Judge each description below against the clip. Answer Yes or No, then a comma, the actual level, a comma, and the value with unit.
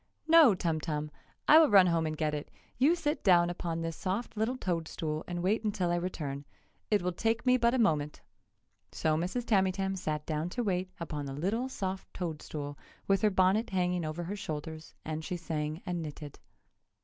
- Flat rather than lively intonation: No, average, 4.7 semitones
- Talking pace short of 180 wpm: No, average, 195 wpm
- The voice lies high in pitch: No, medium, 175 Hz